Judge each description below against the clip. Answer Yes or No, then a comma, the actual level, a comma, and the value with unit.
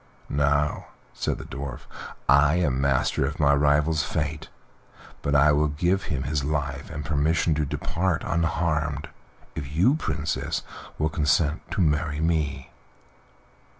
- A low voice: Yes, very low, 75 Hz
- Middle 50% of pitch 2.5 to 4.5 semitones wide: No, narrow, 2.0 semitones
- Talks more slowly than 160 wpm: Yes, slow, 135 wpm